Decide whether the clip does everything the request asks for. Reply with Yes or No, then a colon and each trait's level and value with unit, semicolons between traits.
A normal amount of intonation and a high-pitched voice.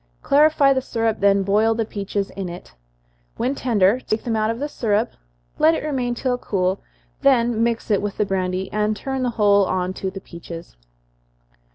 Yes: average, 3.9 semitones; high, 215 Hz